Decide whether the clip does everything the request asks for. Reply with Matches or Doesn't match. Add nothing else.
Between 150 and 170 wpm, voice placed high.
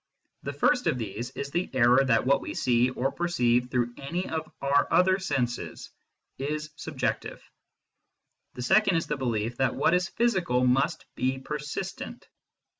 Doesn't match